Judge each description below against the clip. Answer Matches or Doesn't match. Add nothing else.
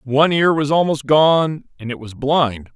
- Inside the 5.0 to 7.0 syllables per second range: Doesn't match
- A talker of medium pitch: Matches